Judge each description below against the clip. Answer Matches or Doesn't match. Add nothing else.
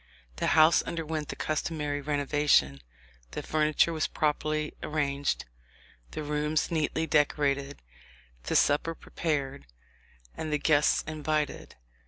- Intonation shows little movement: Matches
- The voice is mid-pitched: Matches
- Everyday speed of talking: Doesn't match